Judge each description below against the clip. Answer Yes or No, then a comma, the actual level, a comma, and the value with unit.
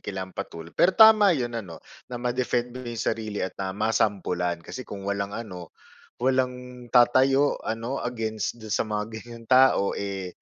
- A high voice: No, low, 115 Hz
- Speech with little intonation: No, average, 4.0 semitones